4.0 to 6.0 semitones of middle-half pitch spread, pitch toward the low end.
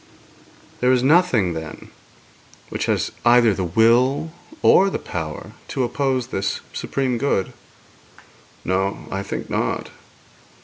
Yes: wide, 5.5 semitones; low, 120 Hz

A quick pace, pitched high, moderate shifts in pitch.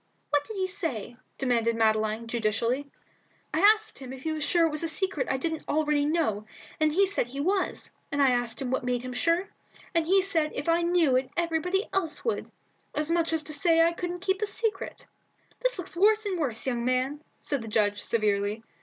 No: fast, 215 wpm; very high, 305 Hz; wide, 6.0 semitones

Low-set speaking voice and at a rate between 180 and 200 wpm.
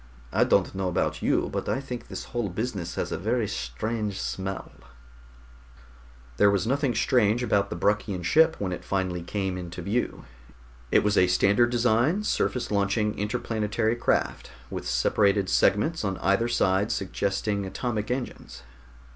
No: low, 105 Hz; average, 150 wpm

